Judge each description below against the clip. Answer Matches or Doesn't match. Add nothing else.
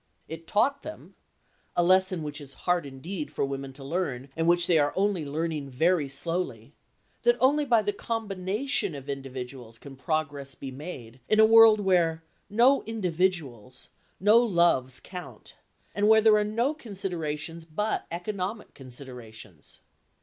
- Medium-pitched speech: Matches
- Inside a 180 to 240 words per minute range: Doesn't match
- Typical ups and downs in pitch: Doesn't match